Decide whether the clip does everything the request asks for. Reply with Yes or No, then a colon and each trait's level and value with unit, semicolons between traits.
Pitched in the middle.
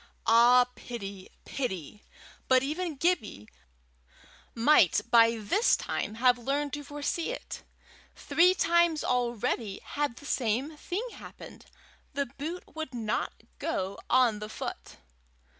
No: very high, 255 Hz